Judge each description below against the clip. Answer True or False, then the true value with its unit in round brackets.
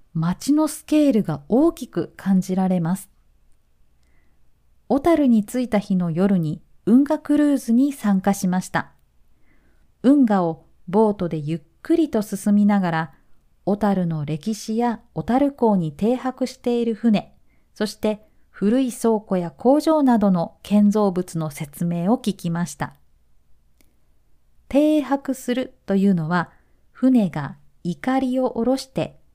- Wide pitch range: True (7.1 semitones)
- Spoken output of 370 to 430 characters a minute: False (235 characters per minute)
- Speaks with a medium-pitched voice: False (205 Hz)